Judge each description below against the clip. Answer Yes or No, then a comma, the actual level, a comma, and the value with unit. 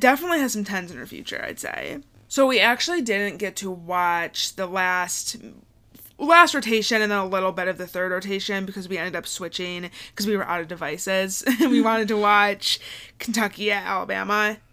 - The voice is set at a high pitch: Yes, high, 200 Hz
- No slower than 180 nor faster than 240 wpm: Yes, average, 190 wpm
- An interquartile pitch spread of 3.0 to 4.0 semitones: Yes, average, 3.3 semitones